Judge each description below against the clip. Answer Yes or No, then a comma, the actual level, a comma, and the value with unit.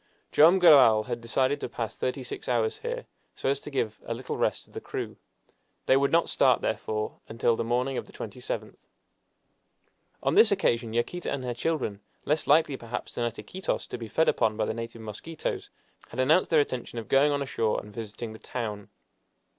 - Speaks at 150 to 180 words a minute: No, average, 195 wpm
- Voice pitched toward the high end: No, low, 120 Hz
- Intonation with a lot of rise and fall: No, average, 3.9 semitones